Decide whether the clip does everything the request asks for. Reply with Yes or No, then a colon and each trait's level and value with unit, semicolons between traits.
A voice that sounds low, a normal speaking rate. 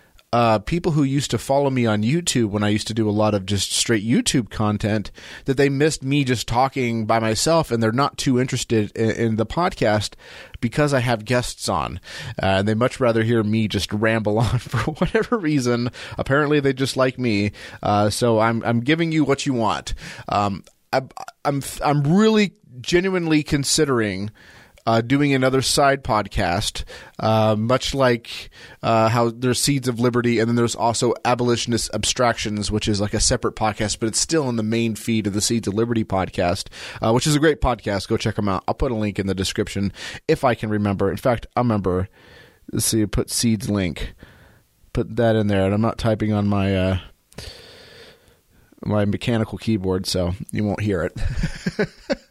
Yes: low, 115 Hz; average, 190 wpm